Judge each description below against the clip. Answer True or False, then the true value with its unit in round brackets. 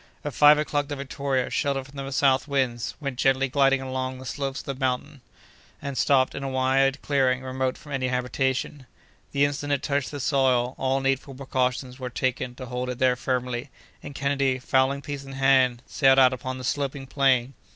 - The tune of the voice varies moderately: False (1.4 semitones)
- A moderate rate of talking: True (195 wpm)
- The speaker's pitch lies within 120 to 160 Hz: True (135 Hz)